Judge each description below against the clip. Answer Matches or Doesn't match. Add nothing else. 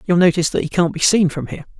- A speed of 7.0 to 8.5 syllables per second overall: Matches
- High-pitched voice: Doesn't match